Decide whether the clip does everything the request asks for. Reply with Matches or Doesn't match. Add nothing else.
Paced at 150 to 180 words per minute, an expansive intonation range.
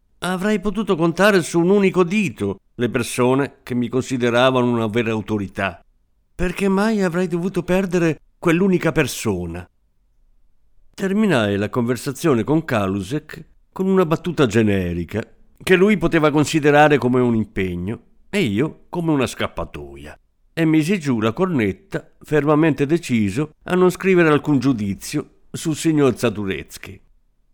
Doesn't match